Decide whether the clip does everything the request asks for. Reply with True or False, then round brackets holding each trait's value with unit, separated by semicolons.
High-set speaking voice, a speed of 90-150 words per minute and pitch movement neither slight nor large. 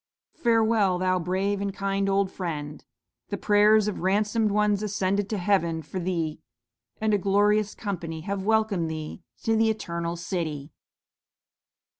True (195 Hz; 140 wpm; 3.4 semitones)